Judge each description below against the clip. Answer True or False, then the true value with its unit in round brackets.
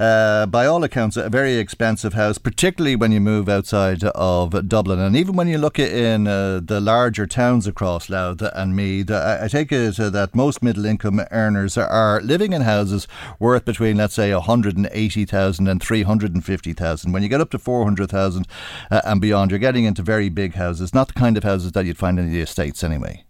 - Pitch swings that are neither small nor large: True (3.2 semitones)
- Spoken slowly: False (190 wpm)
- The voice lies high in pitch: False (105 Hz)